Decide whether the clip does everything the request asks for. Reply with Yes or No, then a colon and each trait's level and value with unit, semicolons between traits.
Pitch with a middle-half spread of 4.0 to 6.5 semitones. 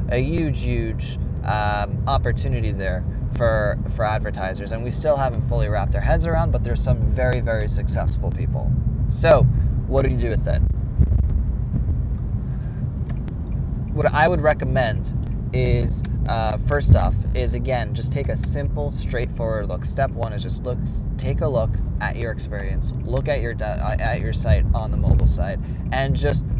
Yes: average, 4.6 semitones